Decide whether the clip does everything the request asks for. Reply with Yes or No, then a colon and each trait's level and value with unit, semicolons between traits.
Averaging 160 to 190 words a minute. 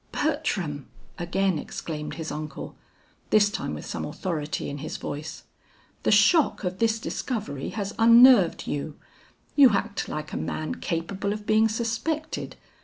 No: average, 140 wpm